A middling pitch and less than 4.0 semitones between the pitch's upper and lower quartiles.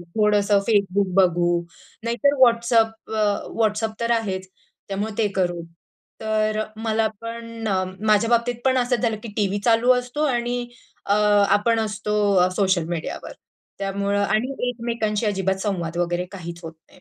No: high, 215 Hz; average, 2.9 semitones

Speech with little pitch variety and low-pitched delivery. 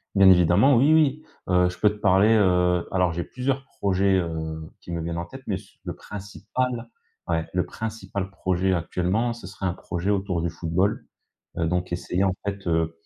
No: average, 3.0 semitones; very low, 95 Hz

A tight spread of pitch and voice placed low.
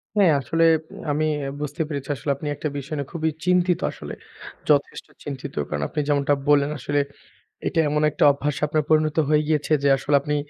No: narrow, 1.7 semitones; medium, 150 Hz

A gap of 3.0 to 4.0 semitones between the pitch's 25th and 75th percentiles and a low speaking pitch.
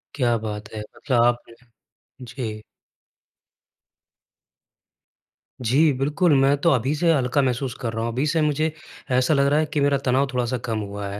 Yes: average, 3.7 semitones; low, 130 Hz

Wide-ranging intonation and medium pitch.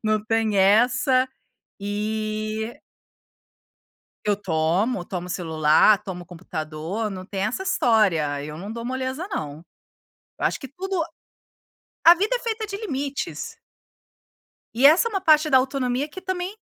No: wide, 7.3 semitones; high, 220 Hz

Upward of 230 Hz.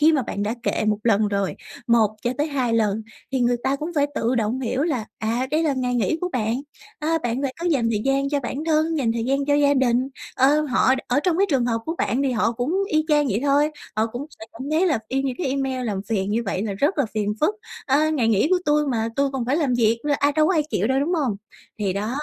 Yes: very high, 260 Hz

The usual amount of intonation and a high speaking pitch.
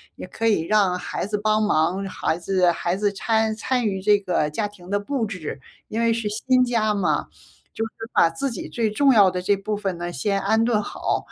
Yes: average, 3.2 semitones; high, 205 Hz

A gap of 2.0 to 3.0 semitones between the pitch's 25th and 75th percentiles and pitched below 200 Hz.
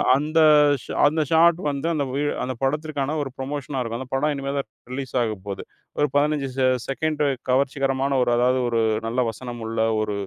Yes: average, 2.7 semitones; low, 135 Hz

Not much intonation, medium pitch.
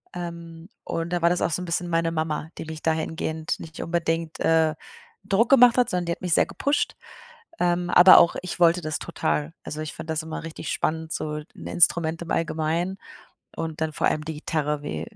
Yes: narrow, 1.7 semitones; medium, 165 Hz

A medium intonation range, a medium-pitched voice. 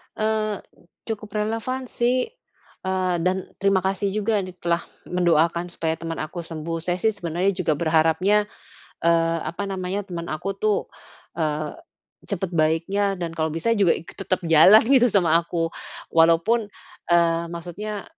Yes: average, 3.6 semitones; medium, 180 Hz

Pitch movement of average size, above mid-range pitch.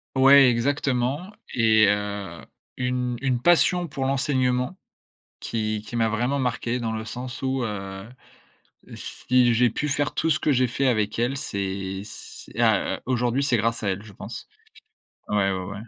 No: average, 3.7 semitones; low, 120 Hz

